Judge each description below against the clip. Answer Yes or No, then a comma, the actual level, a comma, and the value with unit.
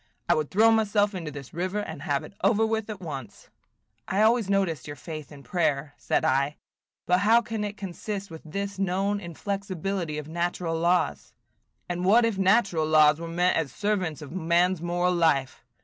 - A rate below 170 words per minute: No, average, 180 wpm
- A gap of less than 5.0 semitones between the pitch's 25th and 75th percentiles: Yes, average, 4.3 semitones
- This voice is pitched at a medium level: Yes, medium, 180 Hz